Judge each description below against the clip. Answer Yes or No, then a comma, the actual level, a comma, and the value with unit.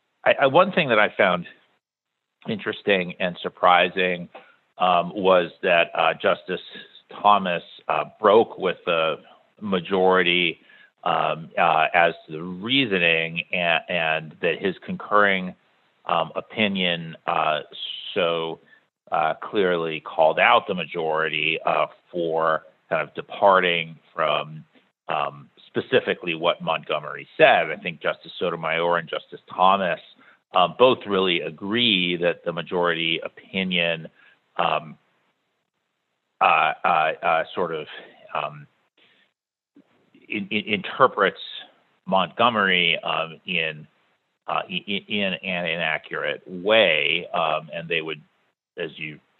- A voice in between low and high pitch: No, very low, 85 Hz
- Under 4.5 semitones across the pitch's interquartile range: Yes, average, 2.9 semitones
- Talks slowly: Yes, slow, 110 wpm